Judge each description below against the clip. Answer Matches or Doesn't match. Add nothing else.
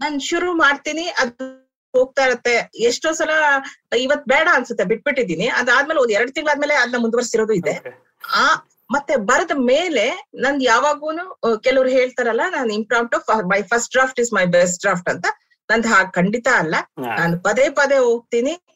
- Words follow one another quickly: Matches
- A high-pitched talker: Matches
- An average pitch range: Matches